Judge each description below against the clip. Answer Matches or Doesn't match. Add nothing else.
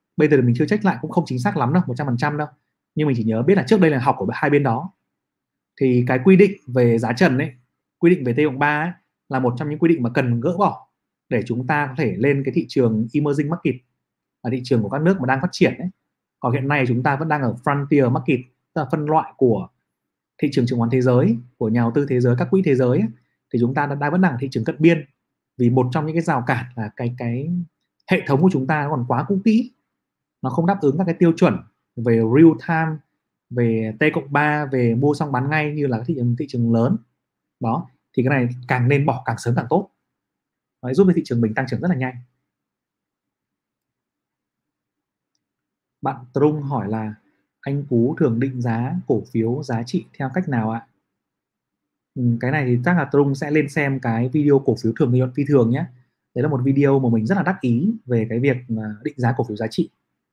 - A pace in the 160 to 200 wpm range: Doesn't match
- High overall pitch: Doesn't match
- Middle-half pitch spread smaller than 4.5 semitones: Matches